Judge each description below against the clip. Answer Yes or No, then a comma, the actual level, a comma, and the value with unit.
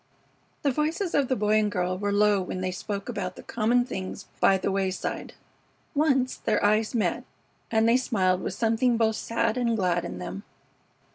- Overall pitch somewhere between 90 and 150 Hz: No, high, 215 Hz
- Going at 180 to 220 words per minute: Yes, average, 185 wpm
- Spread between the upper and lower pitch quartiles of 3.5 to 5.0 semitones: Yes, average, 4.2 semitones